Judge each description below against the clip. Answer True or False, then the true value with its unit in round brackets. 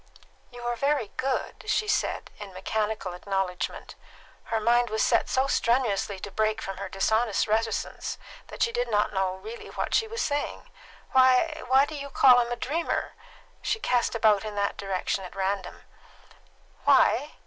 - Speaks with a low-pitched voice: False (225 Hz)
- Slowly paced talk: False (165 wpm)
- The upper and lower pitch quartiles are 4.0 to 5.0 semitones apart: True (4.6 semitones)